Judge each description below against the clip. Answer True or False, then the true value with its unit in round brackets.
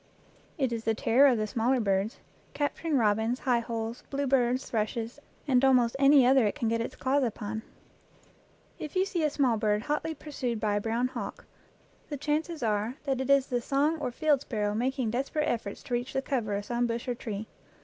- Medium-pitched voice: False (245 Hz)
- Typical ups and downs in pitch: True (3.7 semitones)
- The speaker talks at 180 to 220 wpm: True (200 wpm)